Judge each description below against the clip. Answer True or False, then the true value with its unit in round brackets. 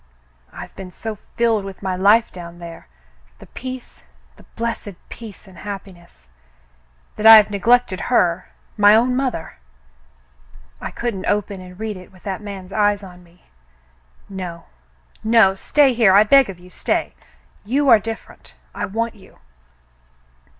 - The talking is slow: False (155 wpm)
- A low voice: False (200 Hz)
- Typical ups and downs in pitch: True (3.6 semitones)